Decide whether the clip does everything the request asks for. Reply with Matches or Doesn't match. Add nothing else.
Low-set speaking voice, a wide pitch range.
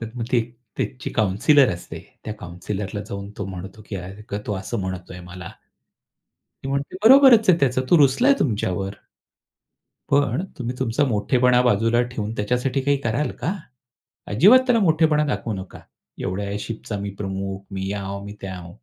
Matches